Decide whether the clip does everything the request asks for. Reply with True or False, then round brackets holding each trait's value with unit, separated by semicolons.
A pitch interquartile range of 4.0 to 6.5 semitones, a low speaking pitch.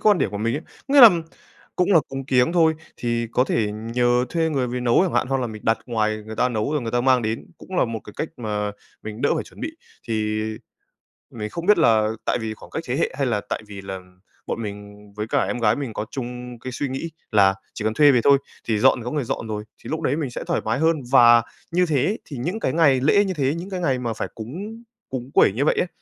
True (5.6 semitones; 125 Hz)